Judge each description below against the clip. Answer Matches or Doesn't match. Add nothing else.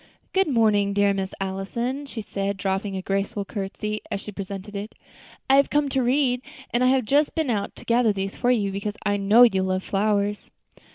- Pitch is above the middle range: Matches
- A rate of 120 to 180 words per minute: Doesn't match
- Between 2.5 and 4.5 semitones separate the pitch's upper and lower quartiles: Matches